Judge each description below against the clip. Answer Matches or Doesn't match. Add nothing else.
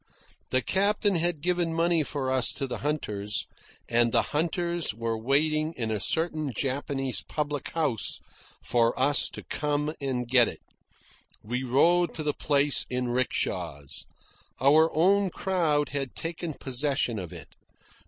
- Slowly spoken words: Doesn't match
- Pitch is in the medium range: Matches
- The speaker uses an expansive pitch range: Doesn't match